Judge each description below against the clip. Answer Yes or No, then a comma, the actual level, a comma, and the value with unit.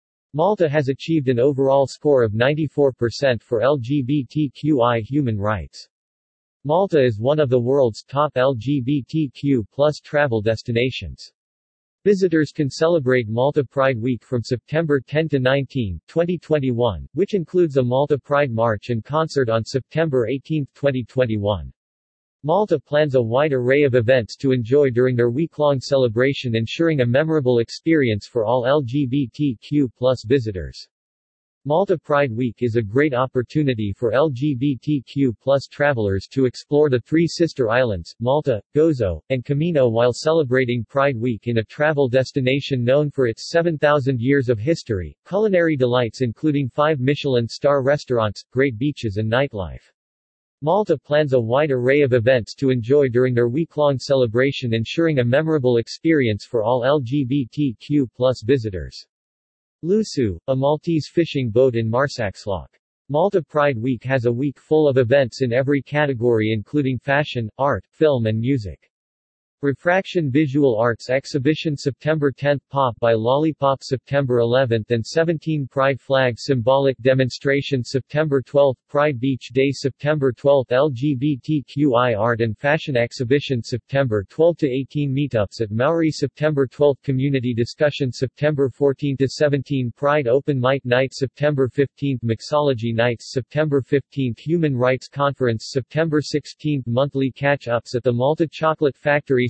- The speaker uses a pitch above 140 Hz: No, low, 135 Hz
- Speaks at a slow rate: Yes, slow, 130 wpm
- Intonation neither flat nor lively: Yes, average, 3.4 semitones